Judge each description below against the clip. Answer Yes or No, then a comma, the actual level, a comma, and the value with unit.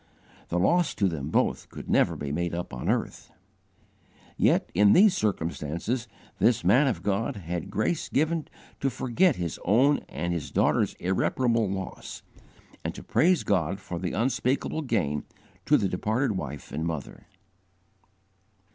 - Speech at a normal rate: Yes, average, 145 wpm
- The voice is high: No, low, 100 Hz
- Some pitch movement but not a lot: No, wide, 7.1 semitones